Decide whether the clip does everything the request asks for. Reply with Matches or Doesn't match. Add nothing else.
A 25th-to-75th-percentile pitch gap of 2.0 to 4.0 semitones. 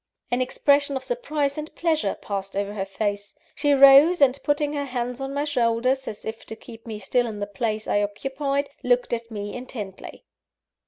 Doesn't match